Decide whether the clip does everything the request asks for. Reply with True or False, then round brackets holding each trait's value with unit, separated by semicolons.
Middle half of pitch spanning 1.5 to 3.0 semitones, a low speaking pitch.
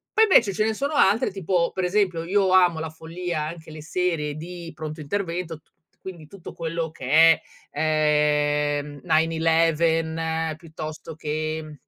False (2.4 semitones; 165 Hz)